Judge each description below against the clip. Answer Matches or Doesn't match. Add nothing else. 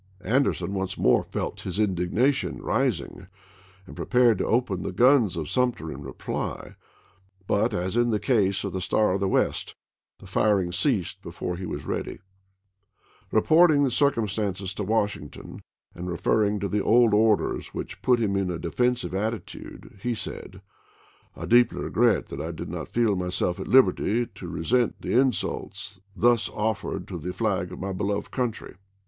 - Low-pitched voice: Matches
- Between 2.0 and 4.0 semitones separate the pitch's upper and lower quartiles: Doesn't match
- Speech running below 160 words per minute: Doesn't match